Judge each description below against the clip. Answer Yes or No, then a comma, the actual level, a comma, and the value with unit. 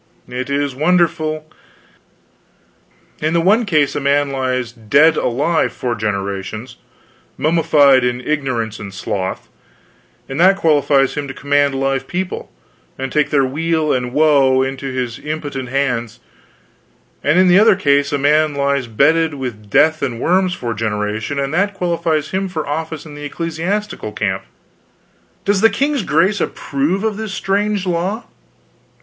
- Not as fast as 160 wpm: Yes, average, 145 wpm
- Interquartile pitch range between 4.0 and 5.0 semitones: Yes, average, 4.4 semitones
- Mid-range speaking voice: Yes, medium, 145 Hz